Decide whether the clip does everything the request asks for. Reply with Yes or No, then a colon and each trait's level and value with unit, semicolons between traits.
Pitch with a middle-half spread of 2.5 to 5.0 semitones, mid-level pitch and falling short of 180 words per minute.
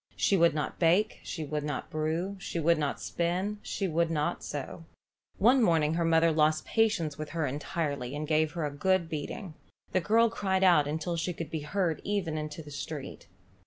No: average, 3.2 semitones; medium, 165 Hz; average, 195 wpm